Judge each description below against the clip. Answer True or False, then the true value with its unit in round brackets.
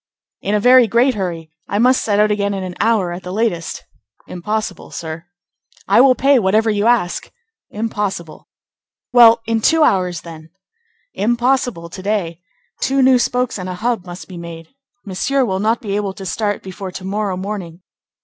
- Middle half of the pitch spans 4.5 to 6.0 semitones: False (4.1 semitones)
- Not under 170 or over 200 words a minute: True (175 wpm)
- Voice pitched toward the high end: True (205 Hz)